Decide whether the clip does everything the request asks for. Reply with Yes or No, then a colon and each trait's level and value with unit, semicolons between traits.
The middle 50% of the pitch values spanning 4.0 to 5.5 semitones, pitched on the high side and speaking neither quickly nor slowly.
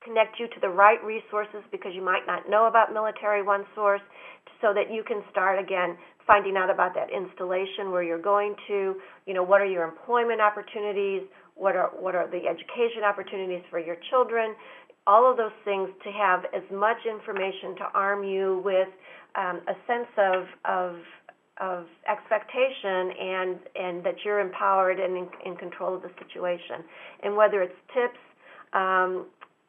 No: narrow, 2.4 semitones; high, 195 Hz; average, 170 wpm